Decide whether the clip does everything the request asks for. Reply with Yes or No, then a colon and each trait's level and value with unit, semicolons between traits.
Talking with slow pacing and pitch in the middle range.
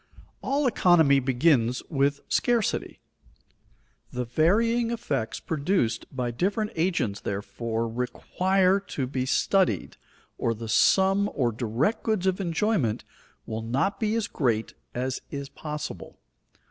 Yes: slow, 120 wpm; medium, 145 Hz